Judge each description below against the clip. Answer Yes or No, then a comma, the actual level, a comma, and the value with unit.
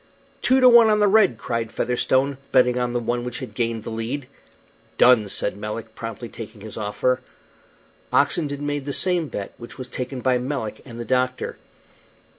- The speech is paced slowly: No, average, 180 wpm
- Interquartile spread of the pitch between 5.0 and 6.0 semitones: No, average, 3.7 semitones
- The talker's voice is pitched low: Yes, low, 125 Hz